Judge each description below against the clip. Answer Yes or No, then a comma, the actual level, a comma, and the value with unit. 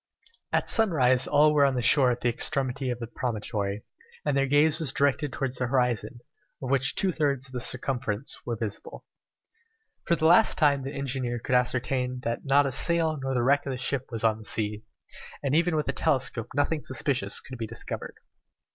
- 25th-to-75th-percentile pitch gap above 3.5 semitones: No, average, 2.7 semitones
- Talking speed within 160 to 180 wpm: No, average, 200 wpm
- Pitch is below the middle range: Yes, low, 130 Hz